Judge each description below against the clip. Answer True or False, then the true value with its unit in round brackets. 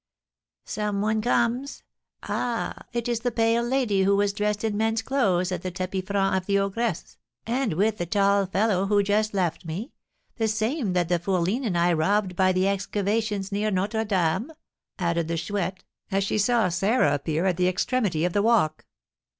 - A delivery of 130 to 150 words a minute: False (185 wpm)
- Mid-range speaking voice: False (200 Hz)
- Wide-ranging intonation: False (3.3 semitones)